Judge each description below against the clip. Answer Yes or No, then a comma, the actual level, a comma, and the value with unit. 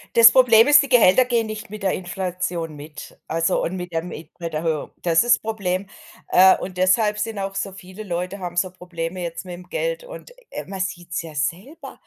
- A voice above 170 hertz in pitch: Yes, medium, 185 Hz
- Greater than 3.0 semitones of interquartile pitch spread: Yes, average, 3.8 semitones